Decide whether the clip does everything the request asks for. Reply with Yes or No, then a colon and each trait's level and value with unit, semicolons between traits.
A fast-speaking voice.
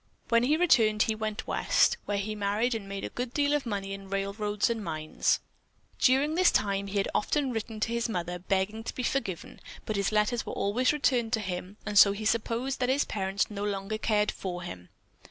Yes: fast, 210 wpm